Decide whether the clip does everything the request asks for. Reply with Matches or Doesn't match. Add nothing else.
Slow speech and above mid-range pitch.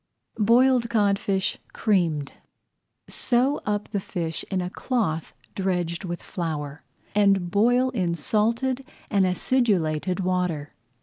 Matches